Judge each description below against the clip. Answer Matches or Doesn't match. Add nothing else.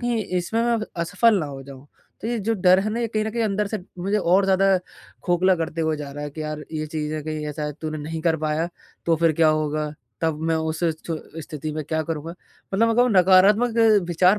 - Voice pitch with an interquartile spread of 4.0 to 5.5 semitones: Matches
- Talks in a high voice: Doesn't match